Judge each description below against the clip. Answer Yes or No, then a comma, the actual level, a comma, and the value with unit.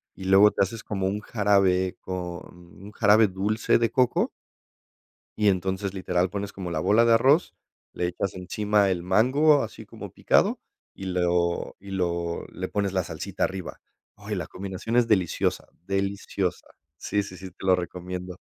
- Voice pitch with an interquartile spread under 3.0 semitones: Yes, narrow, 2.4 semitones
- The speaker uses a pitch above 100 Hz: No, very low, 95 Hz